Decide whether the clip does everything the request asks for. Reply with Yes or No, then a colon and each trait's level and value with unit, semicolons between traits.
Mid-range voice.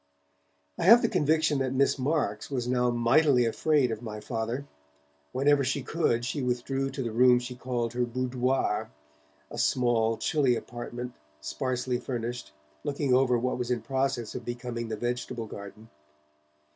No: low, 125 Hz